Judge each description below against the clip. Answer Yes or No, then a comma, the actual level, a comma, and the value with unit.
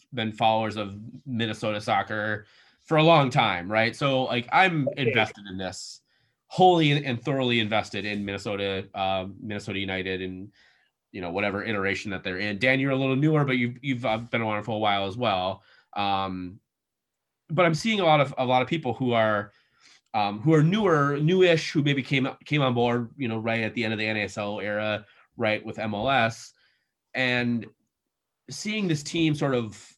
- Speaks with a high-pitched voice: No, low, 115 Hz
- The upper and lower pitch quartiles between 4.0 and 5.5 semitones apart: Yes, average, 4.7 semitones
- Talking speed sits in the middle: Yes, average, 185 wpm